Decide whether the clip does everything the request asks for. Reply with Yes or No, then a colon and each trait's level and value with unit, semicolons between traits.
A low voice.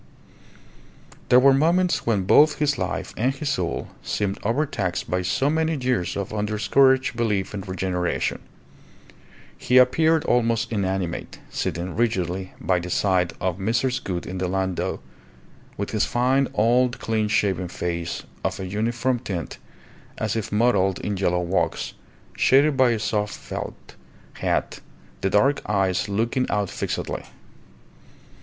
Yes: low, 105 Hz